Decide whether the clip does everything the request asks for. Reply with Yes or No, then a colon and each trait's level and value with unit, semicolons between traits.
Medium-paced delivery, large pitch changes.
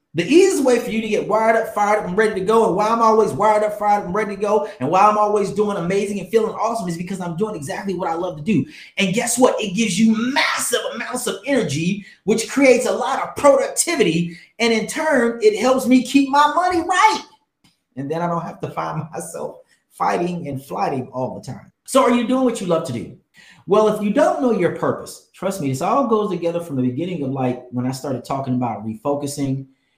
No: fast, 240 wpm; wide, 6.3 semitones